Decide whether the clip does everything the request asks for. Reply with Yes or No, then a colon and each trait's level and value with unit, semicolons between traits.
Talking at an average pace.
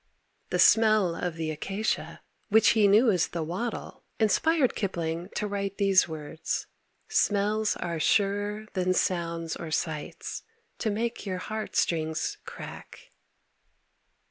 No: slow, 125 wpm